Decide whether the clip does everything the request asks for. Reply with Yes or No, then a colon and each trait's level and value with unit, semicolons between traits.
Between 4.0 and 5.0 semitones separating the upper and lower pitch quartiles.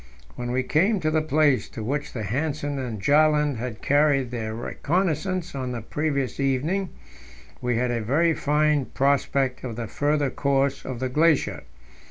No: average, 3.4 semitones